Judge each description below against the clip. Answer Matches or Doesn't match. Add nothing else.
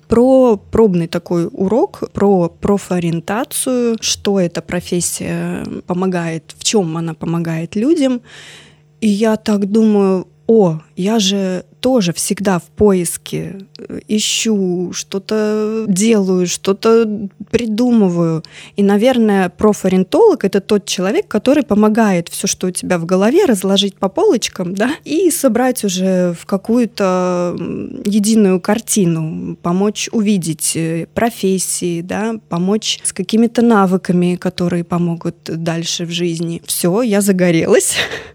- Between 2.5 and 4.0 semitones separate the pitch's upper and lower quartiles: Matches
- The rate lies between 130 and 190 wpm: Doesn't match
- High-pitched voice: Matches